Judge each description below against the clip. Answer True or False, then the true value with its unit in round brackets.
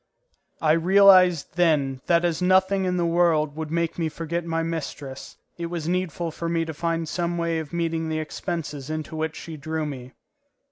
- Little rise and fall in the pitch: True (1.6 semitones)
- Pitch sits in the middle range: True (165 Hz)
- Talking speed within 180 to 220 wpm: True (185 wpm)